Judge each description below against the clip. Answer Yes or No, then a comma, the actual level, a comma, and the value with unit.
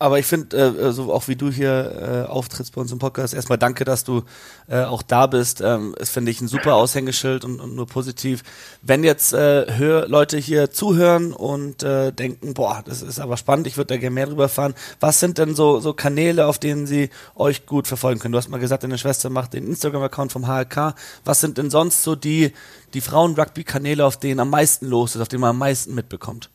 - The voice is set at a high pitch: No, low, 135 Hz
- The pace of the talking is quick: Yes, fast, 225 wpm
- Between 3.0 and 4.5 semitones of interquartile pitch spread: No, narrow, 2.4 semitones